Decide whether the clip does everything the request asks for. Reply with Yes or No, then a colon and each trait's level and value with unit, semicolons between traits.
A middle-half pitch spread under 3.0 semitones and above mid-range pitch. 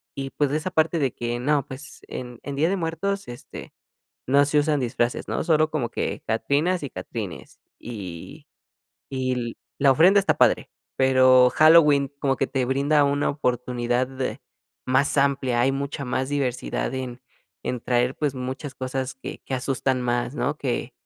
No: narrow, 2.6 semitones; low, 135 Hz